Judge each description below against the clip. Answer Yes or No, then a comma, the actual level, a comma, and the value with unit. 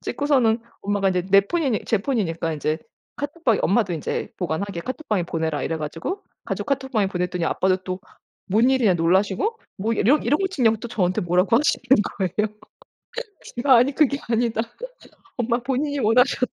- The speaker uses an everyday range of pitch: No, wide, 6.2 semitones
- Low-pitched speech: No, high, 220 Hz